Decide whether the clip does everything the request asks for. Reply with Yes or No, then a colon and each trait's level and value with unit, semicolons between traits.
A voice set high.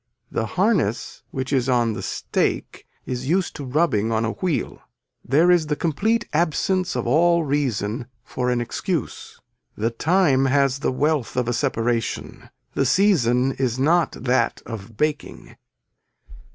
No: low, 135 Hz